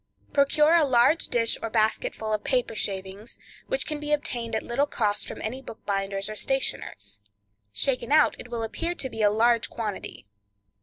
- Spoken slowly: No, average, 170 wpm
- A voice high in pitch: Yes, high, 230 Hz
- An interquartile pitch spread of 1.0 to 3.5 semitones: No, average, 4.4 semitones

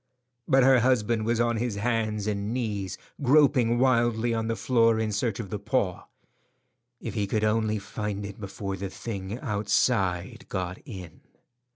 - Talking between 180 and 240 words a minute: No, average, 160 wpm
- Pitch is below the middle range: Yes, low, 110 Hz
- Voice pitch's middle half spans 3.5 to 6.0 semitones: No, average, 2.9 semitones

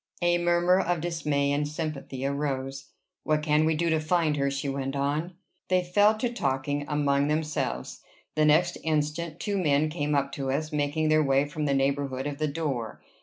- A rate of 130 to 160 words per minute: No, average, 185 wpm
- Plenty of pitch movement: No, narrow, 2.5 semitones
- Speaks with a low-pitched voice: No, medium, 150 Hz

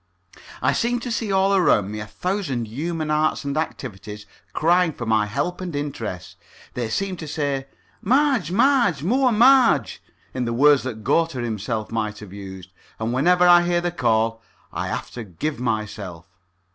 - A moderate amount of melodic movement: No, wide, 8.3 semitones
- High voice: No, medium, 140 Hz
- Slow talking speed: No, average, 170 wpm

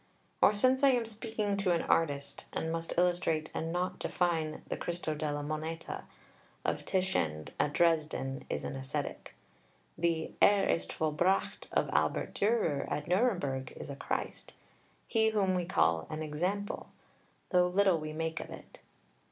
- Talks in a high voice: No, medium, 165 Hz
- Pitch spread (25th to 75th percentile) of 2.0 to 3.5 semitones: No, average, 4.1 semitones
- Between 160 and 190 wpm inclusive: No, average, 150 wpm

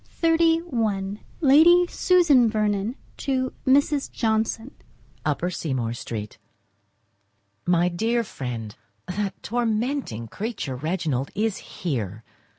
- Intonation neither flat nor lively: No, wide, 8.9 semitones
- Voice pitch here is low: No, high, 215 Hz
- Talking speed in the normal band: No, slow, 85 wpm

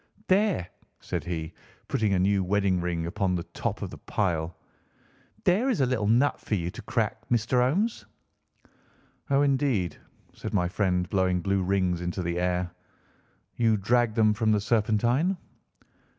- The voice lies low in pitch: Yes, low, 100 Hz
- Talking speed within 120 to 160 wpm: Yes, average, 155 wpm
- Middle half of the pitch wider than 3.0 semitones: Yes, average, 5.2 semitones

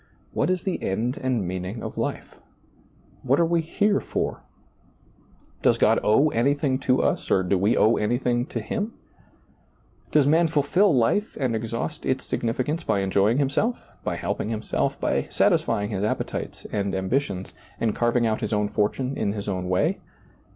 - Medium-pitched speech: No, low, 120 Hz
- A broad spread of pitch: Yes, wide, 5.7 semitones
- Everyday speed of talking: Yes, average, 165 wpm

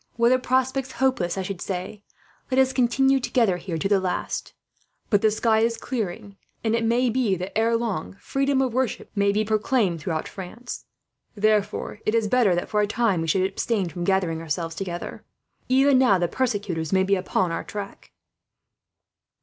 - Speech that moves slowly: No, average, 180 wpm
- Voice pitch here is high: Yes, high, 210 Hz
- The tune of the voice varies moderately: Yes, average, 4.7 semitones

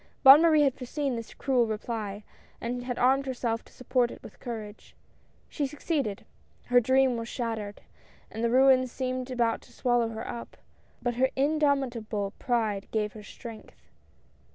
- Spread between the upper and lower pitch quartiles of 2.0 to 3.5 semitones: Yes, average, 2.8 semitones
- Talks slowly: No, average, 160 wpm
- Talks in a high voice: Yes, high, 245 Hz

